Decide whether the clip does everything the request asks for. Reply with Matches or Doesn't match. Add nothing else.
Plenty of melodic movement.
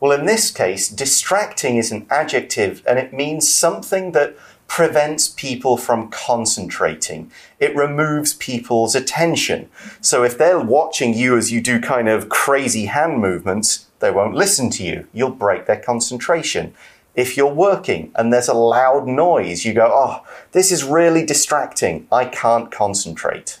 Doesn't match